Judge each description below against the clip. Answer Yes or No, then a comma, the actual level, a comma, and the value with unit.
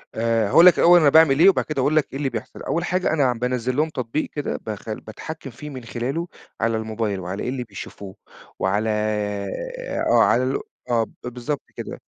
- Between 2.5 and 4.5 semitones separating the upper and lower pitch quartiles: No, average, 4.9 semitones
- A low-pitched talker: Yes, low, 125 Hz